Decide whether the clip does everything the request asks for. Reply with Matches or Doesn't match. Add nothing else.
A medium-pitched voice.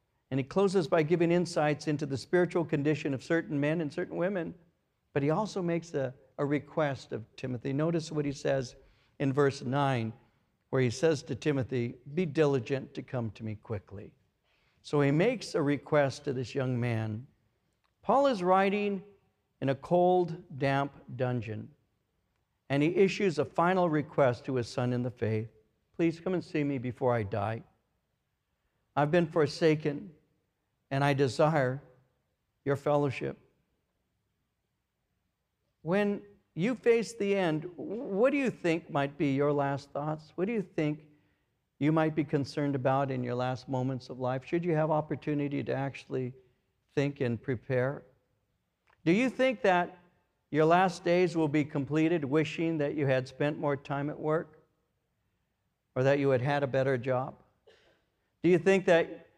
Matches